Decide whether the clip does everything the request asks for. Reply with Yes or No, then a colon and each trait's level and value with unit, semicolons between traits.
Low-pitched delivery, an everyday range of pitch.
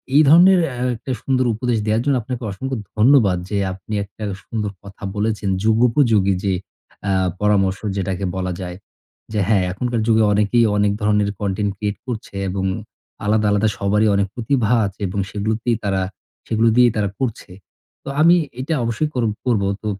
Yes: low, 110 Hz; average, 3.3 semitones